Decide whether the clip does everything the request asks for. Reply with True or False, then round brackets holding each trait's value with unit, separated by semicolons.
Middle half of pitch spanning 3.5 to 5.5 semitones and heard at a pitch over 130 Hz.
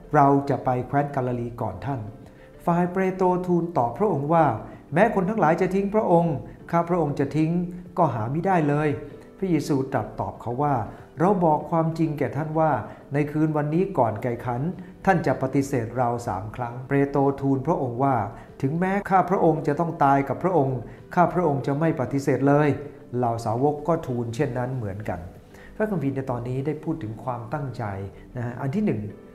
True (5.0 semitones; 140 Hz)